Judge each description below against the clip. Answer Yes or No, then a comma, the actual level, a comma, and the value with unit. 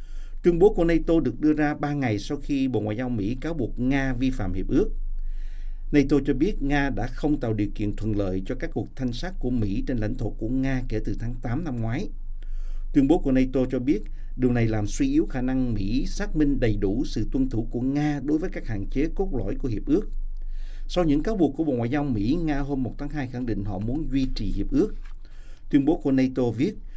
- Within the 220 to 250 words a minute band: Yes, average, 245 wpm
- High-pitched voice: No, low, 130 Hz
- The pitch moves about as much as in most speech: Yes, average, 4.9 semitones